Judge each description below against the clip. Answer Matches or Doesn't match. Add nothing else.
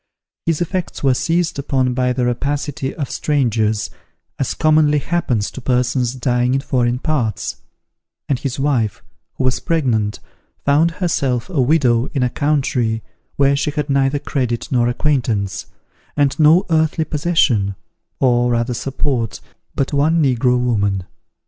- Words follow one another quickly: Doesn't match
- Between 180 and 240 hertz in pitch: Doesn't match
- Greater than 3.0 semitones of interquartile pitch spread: Matches